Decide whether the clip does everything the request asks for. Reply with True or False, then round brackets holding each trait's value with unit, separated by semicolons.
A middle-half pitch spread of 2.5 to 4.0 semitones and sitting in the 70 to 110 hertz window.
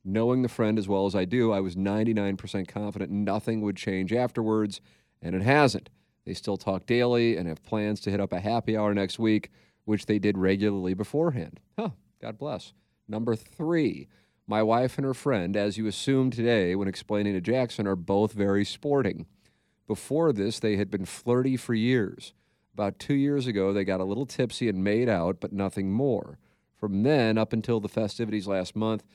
True (3.1 semitones; 105 Hz)